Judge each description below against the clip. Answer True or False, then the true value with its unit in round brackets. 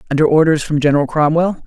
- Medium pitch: True (155 Hz)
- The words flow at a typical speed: True (180 wpm)